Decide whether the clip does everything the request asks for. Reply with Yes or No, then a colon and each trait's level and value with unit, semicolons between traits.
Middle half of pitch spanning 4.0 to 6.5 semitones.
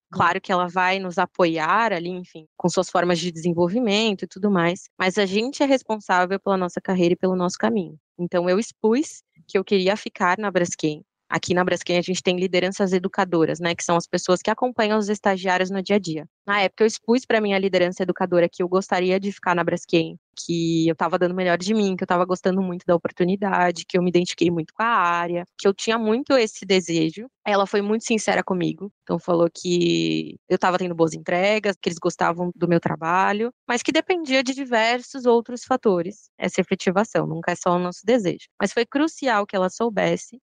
No: average, 3.1 semitones